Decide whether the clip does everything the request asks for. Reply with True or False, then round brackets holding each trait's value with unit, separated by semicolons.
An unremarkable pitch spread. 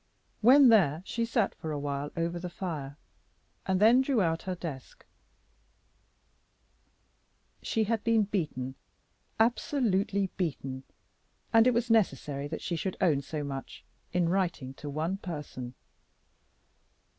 False (7.0 semitones)